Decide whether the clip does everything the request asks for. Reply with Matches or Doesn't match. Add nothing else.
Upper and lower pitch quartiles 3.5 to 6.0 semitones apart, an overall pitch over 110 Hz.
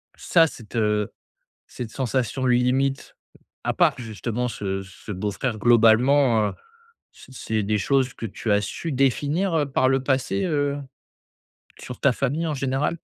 Matches